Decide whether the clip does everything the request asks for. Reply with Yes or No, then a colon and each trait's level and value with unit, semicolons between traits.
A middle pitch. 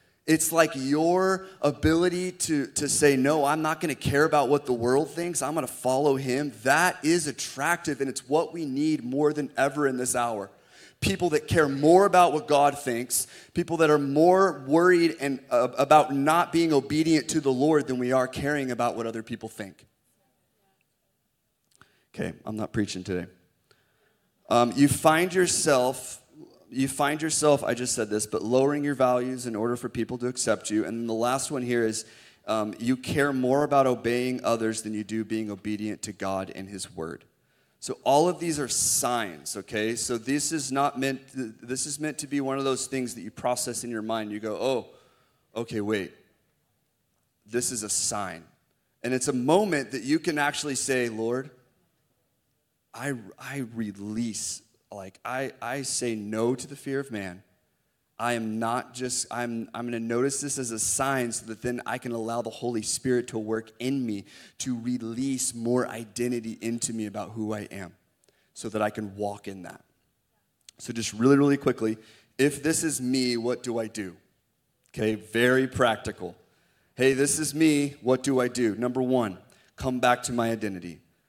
No: low, 125 Hz